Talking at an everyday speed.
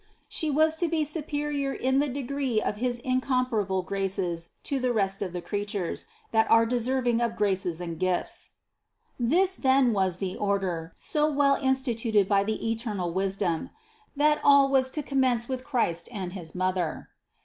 Yes: average, 165 wpm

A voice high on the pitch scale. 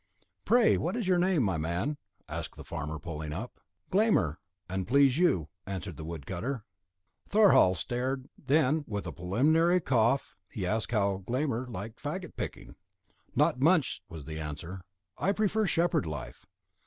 No: low, 120 Hz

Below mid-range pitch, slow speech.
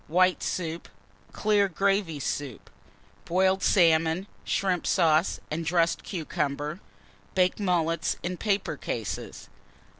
No: medium, 170 Hz; slow, 100 wpm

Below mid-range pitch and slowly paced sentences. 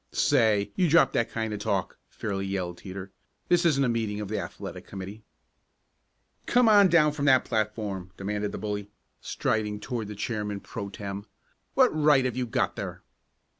No: low, 110 Hz; average, 170 wpm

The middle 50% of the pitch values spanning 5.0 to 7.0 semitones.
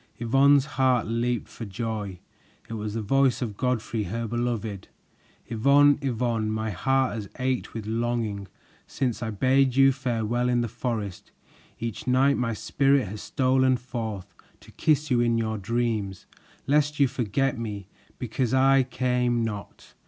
No: average, 3.1 semitones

